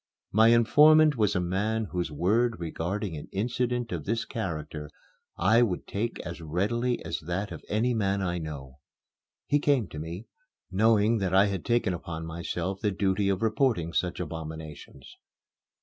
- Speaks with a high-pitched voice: No, very low, 95 Hz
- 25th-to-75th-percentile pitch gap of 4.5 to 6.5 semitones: Yes, average, 5.1 semitones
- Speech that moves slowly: No, average, 160 wpm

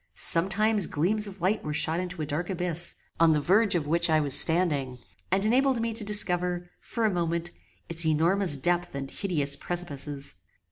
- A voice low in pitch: No, medium, 175 Hz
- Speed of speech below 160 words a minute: No, average, 180 wpm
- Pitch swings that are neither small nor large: Yes, average, 3.9 semitones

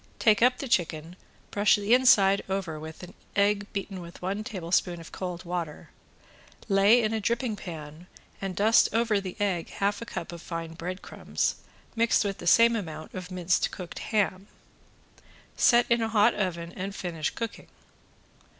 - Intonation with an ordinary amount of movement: Yes, average, 3.7 semitones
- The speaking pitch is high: Yes, high, 195 Hz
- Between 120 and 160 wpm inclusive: No, average, 170 wpm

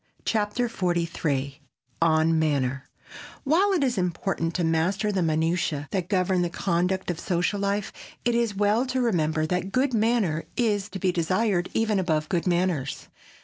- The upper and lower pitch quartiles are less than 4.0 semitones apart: No, average, 4.3 semitones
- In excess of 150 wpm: Yes, average, 160 wpm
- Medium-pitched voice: Yes, medium, 180 Hz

